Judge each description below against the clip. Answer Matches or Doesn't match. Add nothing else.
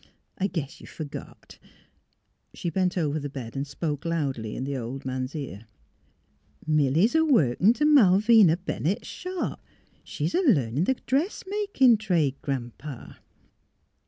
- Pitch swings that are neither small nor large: Doesn't match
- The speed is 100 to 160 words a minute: Matches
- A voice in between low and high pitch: Matches